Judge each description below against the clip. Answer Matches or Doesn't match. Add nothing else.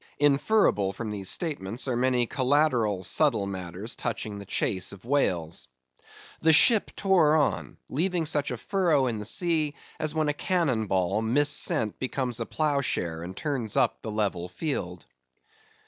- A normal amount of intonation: Doesn't match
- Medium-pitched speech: Doesn't match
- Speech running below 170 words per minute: Matches